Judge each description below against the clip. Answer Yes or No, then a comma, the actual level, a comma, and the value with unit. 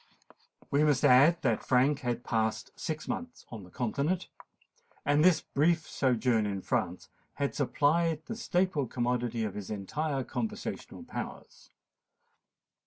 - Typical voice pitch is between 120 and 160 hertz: Yes, low, 135 Hz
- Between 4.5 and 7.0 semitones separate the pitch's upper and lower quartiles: Yes, average, 4.8 semitones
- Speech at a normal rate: No, slow, 130 wpm